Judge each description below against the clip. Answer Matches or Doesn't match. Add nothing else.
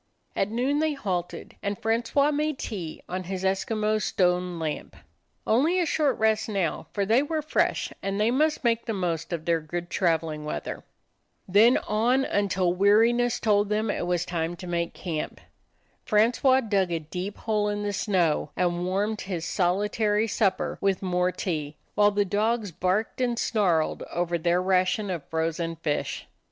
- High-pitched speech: Matches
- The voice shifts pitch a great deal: Doesn't match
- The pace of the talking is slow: Doesn't match